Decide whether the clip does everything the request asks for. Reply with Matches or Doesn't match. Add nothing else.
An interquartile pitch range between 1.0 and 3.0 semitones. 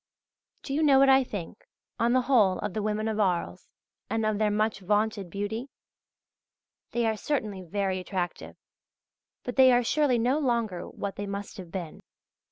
Doesn't match